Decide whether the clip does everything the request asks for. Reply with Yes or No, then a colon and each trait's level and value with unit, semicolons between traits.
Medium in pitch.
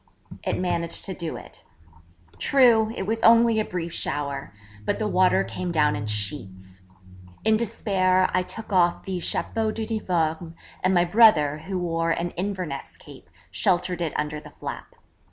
Yes: medium, 180 Hz